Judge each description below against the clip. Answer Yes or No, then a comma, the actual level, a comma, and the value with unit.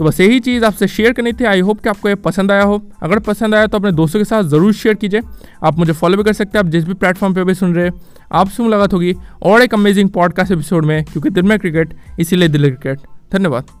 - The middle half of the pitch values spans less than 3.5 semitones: No, average, 3.8 semitones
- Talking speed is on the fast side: Yes, fast, 260 wpm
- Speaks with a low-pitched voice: No, high, 195 Hz